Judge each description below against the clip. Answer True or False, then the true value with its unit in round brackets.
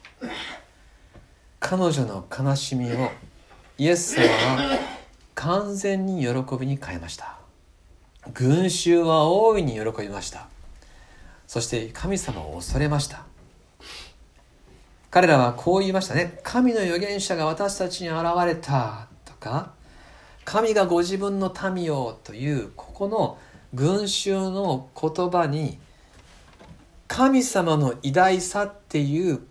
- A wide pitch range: True (7.3 semitones)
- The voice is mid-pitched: True (155 Hz)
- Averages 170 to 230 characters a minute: True (205 characters per minute)